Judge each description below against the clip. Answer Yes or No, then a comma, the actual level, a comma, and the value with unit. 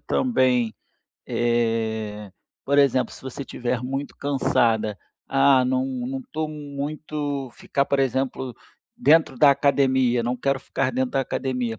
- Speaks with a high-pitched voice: No, low, 130 Hz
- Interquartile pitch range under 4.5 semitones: Yes, narrow, 2.4 semitones